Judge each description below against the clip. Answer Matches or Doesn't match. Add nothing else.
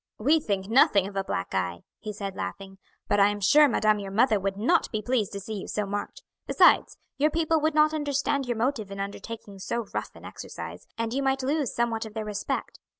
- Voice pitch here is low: Doesn't match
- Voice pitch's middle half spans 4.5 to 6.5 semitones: Matches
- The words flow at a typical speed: Doesn't match